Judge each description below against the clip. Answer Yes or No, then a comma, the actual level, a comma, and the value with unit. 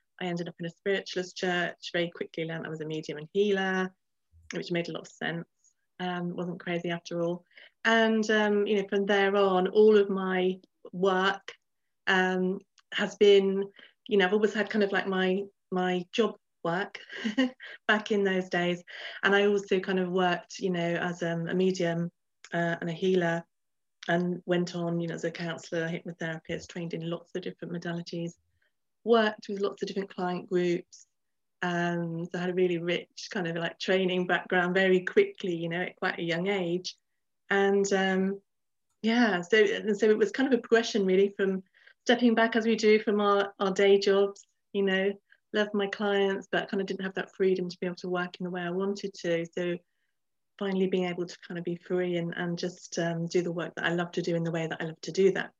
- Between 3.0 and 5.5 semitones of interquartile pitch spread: No, narrow, 2.4 semitones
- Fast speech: Yes, fast, 210 wpm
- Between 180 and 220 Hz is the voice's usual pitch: Yes, medium, 185 Hz